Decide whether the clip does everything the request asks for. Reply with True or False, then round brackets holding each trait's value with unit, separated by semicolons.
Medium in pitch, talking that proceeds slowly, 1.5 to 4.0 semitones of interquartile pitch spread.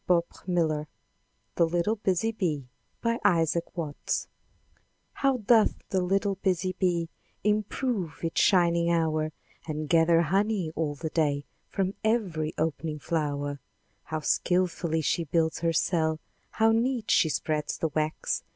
True (170 Hz; 130 wpm; 3.5 semitones)